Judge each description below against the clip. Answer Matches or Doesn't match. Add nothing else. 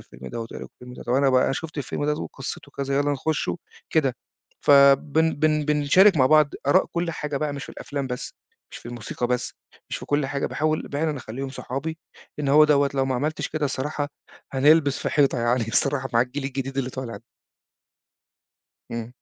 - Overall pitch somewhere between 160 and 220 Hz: Doesn't match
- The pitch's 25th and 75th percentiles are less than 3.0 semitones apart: Matches